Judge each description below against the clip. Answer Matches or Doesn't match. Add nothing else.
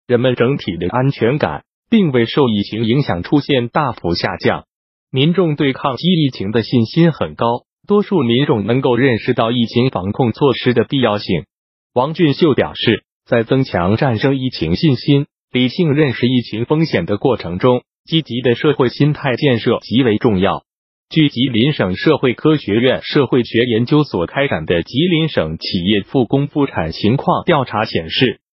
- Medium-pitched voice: Doesn't match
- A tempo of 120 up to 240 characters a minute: Doesn't match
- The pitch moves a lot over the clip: Doesn't match